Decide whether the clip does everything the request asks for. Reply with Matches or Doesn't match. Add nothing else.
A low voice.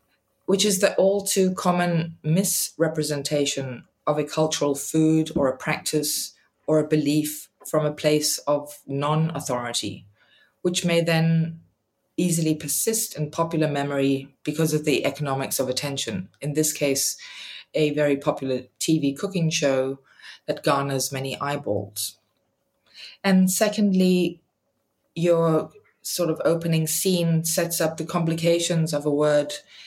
Doesn't match